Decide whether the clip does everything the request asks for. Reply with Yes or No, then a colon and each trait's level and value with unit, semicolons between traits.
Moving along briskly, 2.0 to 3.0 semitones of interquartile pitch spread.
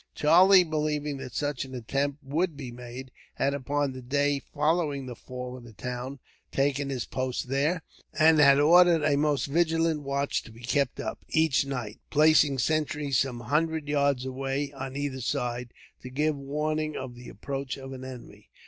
No: average, 175 wpm; narrow, 2.6 semitones